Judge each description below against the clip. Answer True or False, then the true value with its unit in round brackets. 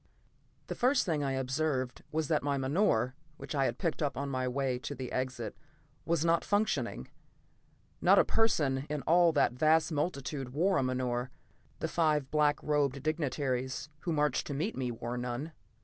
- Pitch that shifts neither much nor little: True (3.5 semitones)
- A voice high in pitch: False (140 Hz)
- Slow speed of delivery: False (175 wpm)